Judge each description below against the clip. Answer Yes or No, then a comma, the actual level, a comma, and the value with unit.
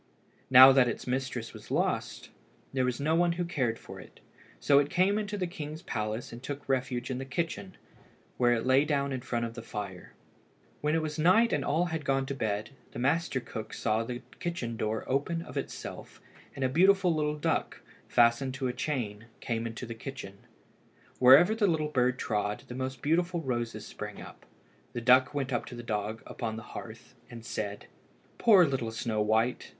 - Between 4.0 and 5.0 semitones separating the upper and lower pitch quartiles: Yes, average, 4.7 semitones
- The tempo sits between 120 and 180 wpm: No, average, 195 wpm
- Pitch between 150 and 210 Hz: No, low, 130 Hz